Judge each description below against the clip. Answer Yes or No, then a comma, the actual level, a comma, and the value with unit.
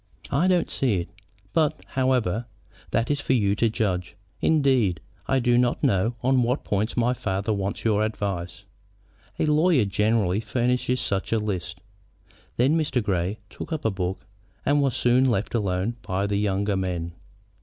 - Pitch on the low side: Yes, low, 110 Hz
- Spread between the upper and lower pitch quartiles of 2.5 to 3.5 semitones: No, average, 4.6 semitones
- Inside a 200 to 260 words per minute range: No, average, 165 wpm